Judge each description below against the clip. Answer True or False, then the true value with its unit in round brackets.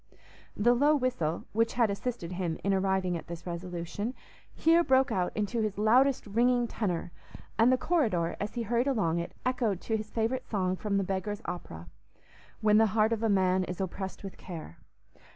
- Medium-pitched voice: False (210 Hz)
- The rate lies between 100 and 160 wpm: False (185 wpm)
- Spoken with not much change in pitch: False (4.5 semitones)